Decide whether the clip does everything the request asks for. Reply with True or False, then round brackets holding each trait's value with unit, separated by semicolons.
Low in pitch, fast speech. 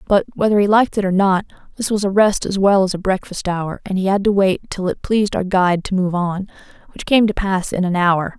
False (190 Hz; 265 wpm)